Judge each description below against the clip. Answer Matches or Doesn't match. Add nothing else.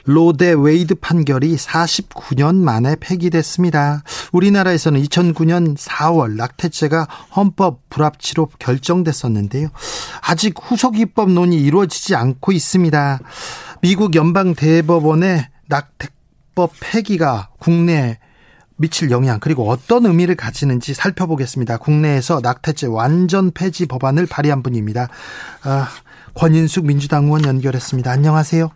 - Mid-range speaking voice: Matches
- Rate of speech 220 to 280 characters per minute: Doesn't match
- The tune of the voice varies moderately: Matches